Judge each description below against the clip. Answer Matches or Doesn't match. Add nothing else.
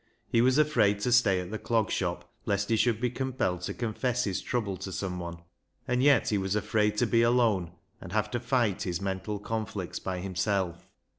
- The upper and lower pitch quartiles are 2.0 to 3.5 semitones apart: Doesn't match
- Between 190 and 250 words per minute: Matches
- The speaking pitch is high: Doesn't match